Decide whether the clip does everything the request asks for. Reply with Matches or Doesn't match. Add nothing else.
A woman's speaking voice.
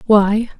Matches